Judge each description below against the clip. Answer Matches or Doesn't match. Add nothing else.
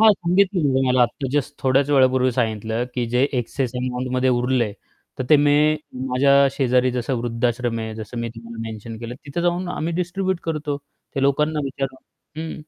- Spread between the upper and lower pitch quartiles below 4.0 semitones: Matches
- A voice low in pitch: Matches